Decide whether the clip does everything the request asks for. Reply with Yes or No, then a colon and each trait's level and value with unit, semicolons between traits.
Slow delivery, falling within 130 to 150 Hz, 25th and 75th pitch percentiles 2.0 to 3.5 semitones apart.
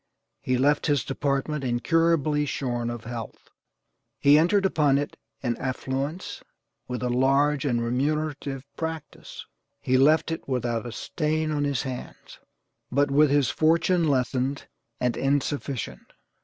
Yes: slow, 130 wpm; medium, 140 Hz; average, 3.0 semitones